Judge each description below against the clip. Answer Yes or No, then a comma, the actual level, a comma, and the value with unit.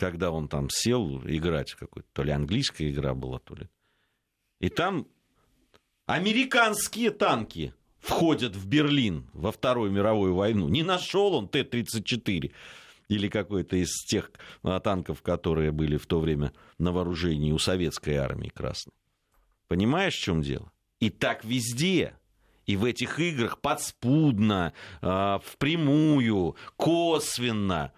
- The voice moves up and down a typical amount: No, wide, 9.0 semitones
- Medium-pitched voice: No, low, 100 Hz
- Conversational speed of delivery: Yes, average, 125 wpm